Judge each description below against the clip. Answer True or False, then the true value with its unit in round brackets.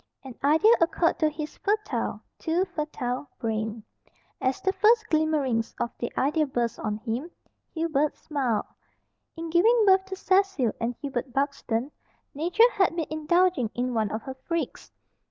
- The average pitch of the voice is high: True (300 Hz)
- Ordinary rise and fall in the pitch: False (6.1 semitones)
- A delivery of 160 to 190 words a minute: False (150 wpm)